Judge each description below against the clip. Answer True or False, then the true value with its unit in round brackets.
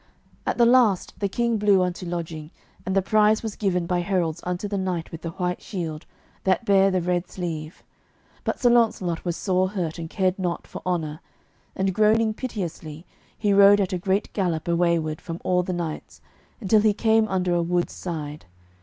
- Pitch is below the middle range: False (185 Hz)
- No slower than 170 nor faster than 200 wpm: True (190 wpm)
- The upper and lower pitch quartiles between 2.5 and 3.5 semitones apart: True (3.0 semitones)